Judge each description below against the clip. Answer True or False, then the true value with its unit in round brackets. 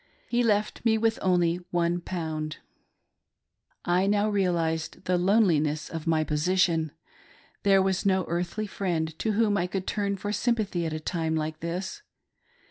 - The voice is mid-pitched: True (180 Hz)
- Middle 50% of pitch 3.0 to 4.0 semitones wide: True (3.7 semitones)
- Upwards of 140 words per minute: True (150 wpm)